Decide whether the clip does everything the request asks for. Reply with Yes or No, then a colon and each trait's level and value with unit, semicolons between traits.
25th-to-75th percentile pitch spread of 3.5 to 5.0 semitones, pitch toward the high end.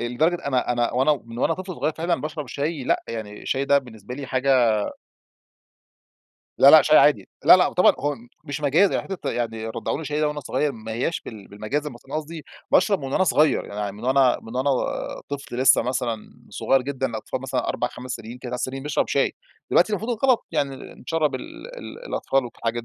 No: average, 4.0 semitones; low, 135 Hz